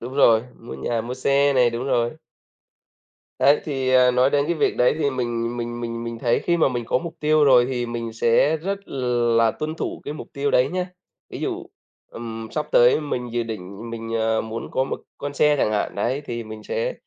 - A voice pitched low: Yes, low, 125 Hz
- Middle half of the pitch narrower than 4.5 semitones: Yes, average, 3.5 semitones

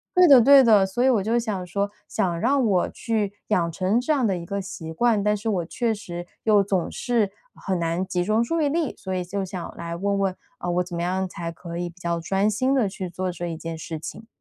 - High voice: Yes, high, 195 Hz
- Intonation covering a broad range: No, average, 4.2 semitones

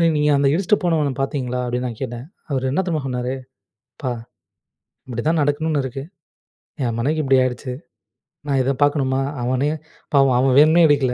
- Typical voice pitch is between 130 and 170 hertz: Yes, low, 135 Hz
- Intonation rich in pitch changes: No, average, 2.8 semitones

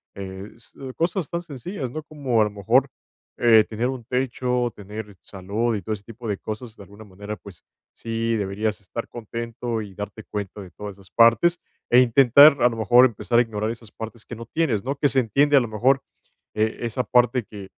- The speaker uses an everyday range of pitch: Yes, average, 3.1 semitones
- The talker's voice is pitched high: No, low, 115 Hz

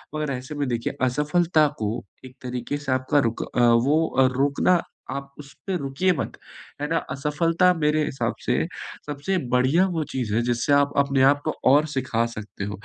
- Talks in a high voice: No, medium, 140 Hz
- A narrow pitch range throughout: No, average, 3.2 semitones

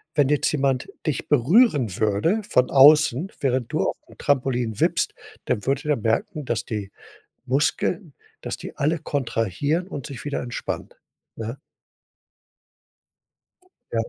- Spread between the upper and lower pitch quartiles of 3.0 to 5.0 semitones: Yes, average, 4.1 semitones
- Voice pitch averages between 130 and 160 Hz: Yes, low, 135 Hz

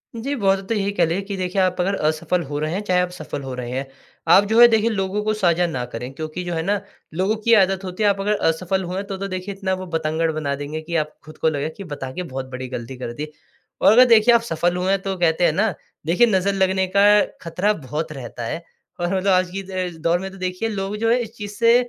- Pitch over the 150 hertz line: Yes, medium, 185 Hz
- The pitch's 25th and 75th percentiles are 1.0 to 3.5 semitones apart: No, average, 3.9 semitones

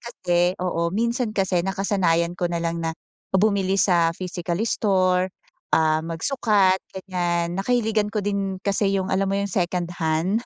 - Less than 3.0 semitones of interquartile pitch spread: Yes, narrow, 2.5 semitones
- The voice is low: No, medium, 185 Hz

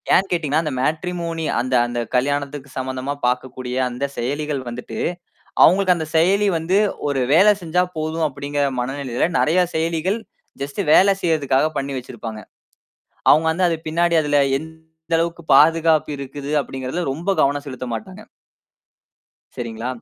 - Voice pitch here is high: No, medium, 150 Hz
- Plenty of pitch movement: No, average, 3.8 semitones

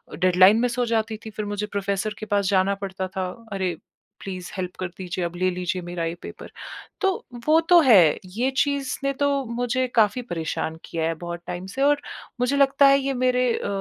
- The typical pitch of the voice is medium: No, high, 205 Hz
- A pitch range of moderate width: No, wide, 5.7 semitones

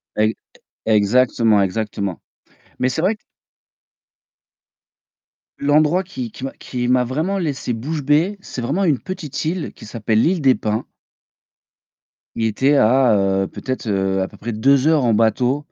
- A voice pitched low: Yes, low, 125 Hz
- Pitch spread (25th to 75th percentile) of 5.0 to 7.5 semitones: Yes, average, 5.3 semitones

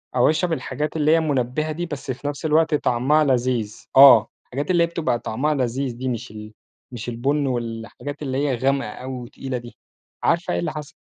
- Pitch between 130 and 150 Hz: Yes, low, 135 Hz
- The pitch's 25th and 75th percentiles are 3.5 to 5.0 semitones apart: Yes, average, 3.9 semitones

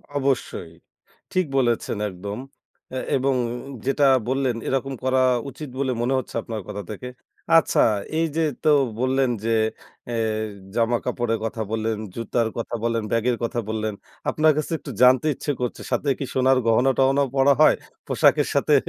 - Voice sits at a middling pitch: No, low, 125 Hz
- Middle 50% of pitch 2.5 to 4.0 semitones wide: Yes, average, 2.8 semitones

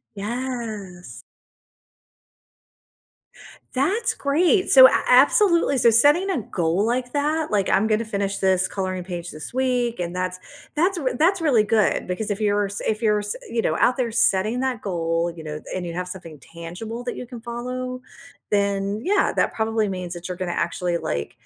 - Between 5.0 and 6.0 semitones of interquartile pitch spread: Yes, wide, 5.5 semitones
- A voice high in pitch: Yes, high, 215 Hz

